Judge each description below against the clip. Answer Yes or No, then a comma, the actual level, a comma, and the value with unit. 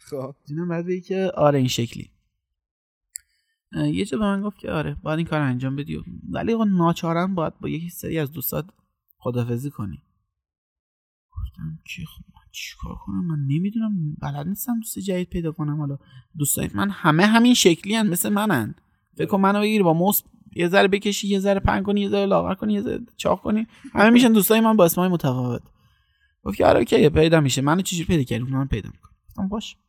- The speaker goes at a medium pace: No, fast, 195 wpm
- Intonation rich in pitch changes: Yes, wide, 7.1 semitones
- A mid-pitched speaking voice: Yes, medium, 165 Hz